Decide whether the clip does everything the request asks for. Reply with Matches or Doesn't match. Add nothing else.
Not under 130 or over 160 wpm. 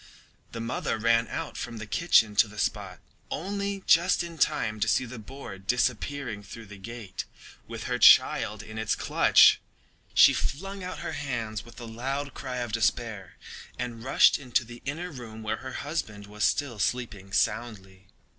Doesn't match